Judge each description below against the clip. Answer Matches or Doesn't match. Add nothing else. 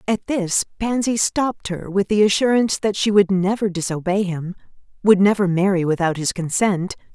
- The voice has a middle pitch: Doesn't match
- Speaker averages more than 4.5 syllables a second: Matches